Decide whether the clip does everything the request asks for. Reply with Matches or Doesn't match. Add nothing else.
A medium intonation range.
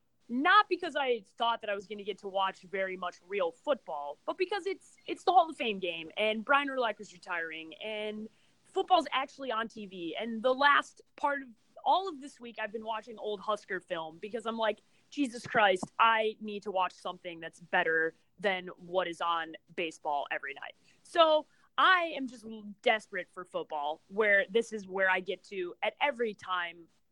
Doesn't match